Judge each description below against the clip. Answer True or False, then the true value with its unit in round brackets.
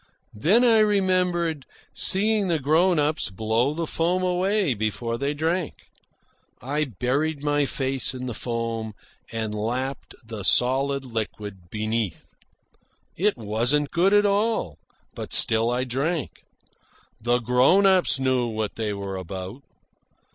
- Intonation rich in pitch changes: True (7.1 semitones)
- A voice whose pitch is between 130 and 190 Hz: True (135 Hz)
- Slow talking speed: True (130 wpm)